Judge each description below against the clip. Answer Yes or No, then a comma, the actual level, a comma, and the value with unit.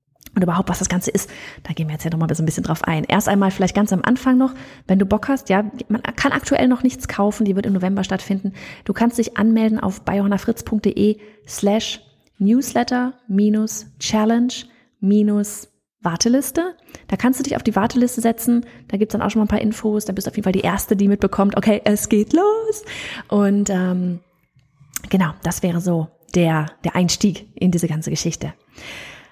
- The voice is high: Yes, high, 205 Hz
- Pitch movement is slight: No, average, 3.5 semitones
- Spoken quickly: Yes, fast, 200 wpm